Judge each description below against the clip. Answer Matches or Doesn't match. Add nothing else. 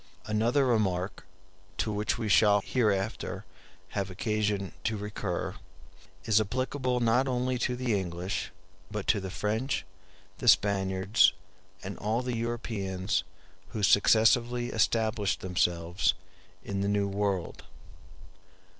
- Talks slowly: Matches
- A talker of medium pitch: Doesn't match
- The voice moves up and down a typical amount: Matches